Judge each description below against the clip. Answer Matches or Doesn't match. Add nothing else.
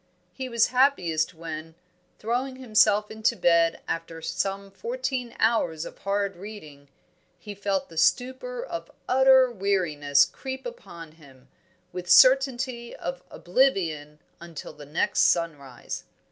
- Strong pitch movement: Matches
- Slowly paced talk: Matches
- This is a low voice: Doesn't match